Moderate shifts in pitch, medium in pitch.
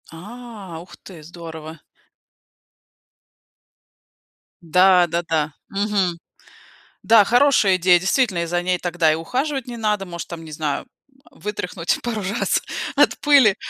Yes: average, 4.2 semitones; medium, 180 Hz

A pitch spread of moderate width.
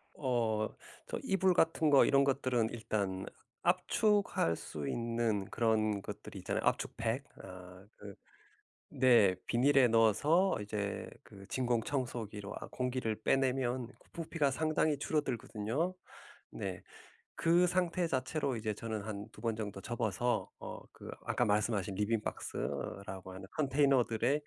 Yes: average, 4.8 semitones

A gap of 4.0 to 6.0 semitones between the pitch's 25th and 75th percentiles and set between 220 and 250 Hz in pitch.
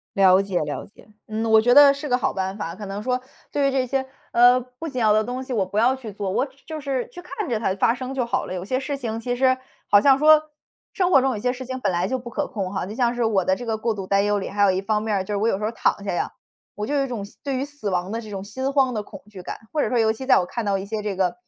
Yes: average, 4.6 semitones; high, 225 Hz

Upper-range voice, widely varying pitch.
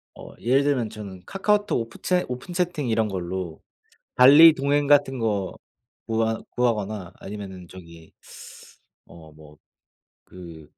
No: low, 110 Hz; wide, 7.2 semitones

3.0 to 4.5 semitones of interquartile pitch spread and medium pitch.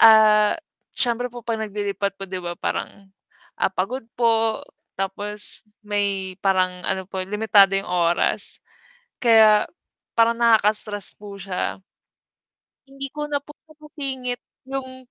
No: average, 3.3 semitones; high, 210 Hz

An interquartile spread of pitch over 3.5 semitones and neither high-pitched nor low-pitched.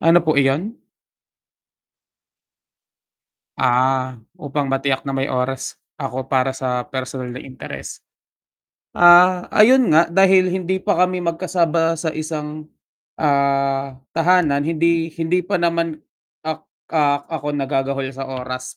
Yes: average, 4.2 semitones; medium, 150 Hz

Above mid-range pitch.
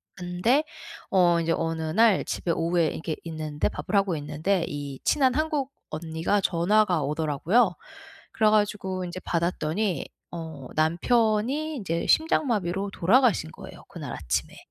No: medium, 180 Hz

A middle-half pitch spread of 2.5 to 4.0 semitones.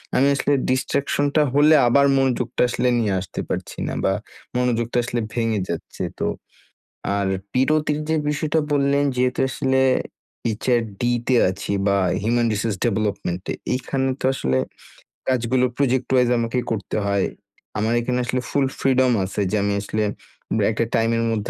Yes: average, 3.5 semitones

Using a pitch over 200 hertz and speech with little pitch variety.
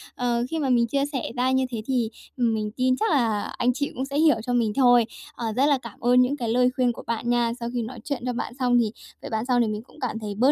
Yes: high, 245 Hz; narrow, 1.9 semitones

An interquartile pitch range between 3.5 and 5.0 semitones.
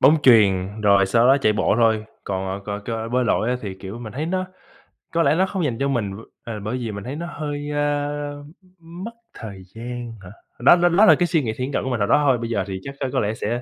No: wide, 5.6 semitones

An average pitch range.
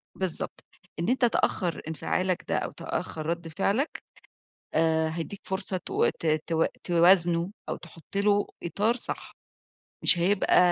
Yes: average, 3.3 semitones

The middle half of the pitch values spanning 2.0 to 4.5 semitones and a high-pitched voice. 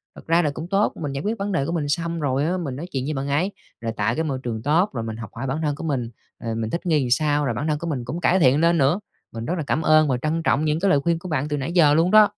No: average, 3.9 semitones; medium, 150 Hz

